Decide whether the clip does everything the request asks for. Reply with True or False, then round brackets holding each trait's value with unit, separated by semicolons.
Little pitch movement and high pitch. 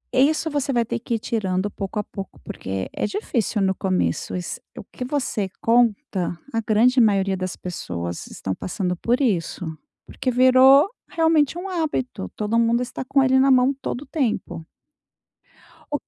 False (5.6 semitones; 230 Hz)